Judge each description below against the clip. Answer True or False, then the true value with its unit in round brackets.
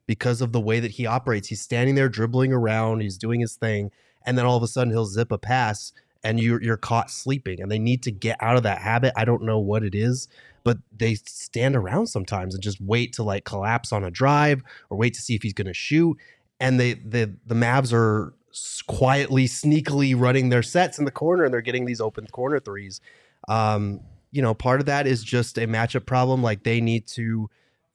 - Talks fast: True (225 wpm)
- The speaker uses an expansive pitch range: False (2.7 semitones)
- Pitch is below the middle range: True (115 Hz)